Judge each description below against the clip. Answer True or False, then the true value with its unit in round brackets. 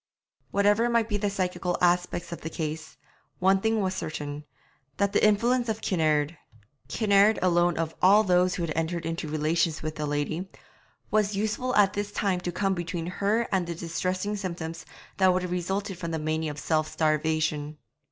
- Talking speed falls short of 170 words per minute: False (180 wpm)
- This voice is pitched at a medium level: True (180 Hz)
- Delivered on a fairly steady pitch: False (3.9 semitones)